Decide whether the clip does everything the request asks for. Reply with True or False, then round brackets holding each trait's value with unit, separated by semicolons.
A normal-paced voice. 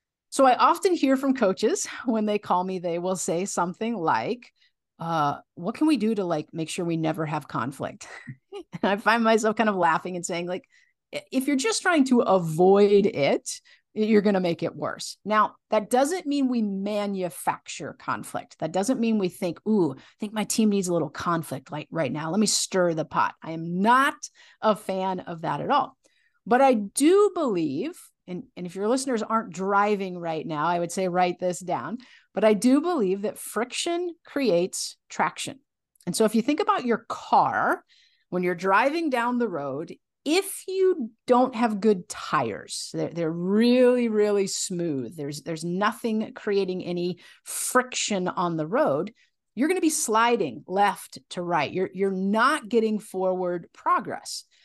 True (180 wpm)